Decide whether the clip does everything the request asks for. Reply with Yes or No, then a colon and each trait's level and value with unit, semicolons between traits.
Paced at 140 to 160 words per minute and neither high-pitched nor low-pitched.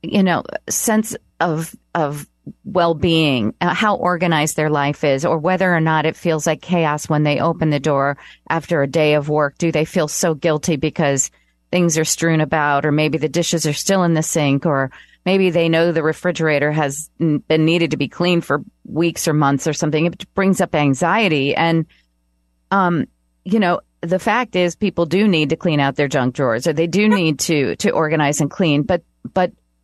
No: average, 195 wpm; medium, 160 Hz